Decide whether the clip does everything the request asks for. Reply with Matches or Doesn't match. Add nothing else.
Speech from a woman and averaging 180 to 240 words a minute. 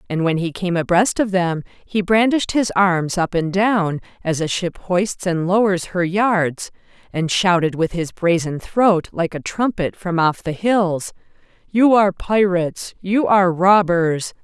Doesn't match